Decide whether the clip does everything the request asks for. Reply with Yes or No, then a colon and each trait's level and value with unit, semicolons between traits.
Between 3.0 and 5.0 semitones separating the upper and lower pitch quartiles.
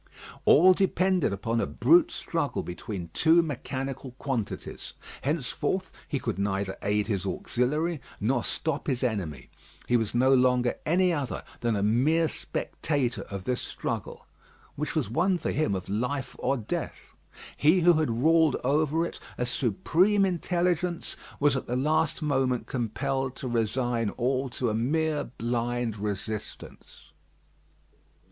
No: wide, 5.4 semitones